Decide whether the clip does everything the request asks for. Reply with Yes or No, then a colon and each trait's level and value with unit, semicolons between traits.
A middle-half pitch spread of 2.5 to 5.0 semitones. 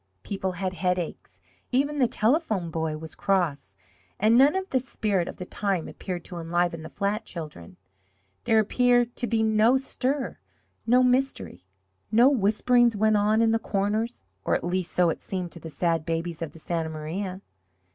No: wide, 5.5 semitones